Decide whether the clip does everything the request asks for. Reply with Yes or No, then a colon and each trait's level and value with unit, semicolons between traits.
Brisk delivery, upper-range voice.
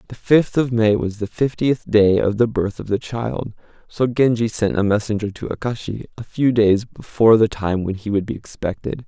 No: fast, 210 wpm; low, 110 Hz